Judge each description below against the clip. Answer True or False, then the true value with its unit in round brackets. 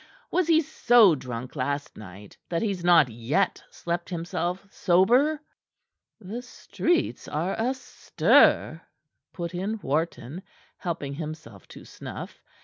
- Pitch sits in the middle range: True (175 Hz)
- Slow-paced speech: True (115 wpm)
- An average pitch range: False (6.4 semitones)